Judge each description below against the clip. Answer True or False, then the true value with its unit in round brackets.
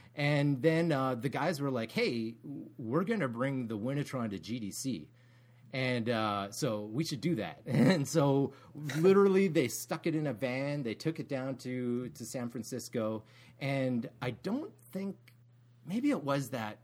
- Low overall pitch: True (130 Hz)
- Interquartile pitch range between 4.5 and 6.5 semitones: False (3.8 semitones)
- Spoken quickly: False (170 wpm)